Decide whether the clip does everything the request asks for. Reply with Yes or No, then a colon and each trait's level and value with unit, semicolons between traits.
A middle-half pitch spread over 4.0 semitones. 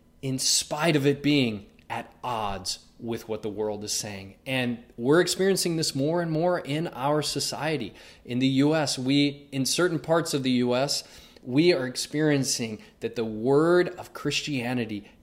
Yes: average, 4.7 semitones